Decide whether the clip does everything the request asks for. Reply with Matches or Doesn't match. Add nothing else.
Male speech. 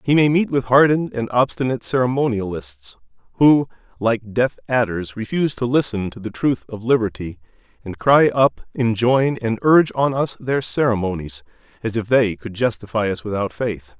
Matches